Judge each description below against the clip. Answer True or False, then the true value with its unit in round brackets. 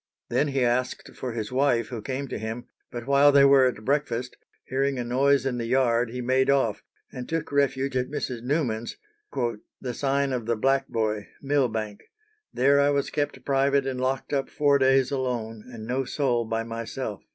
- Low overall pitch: True (130 Hz)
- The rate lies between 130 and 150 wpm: False (185 wpm)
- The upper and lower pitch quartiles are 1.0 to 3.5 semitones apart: True (2.8 semitones)